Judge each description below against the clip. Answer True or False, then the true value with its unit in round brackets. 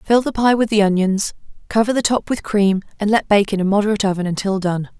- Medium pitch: False (205 Hz)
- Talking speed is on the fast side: True (240 wpm)